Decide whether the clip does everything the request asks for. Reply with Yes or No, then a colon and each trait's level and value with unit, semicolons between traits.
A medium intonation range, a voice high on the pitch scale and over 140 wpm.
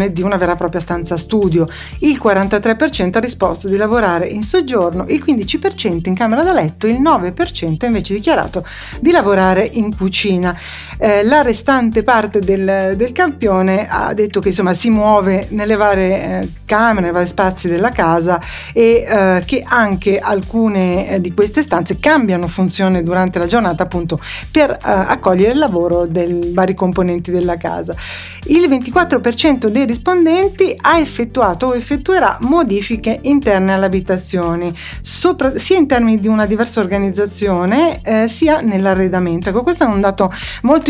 Yes: average, 4.8 semitones; high, 205 Hz; average, 155 wpm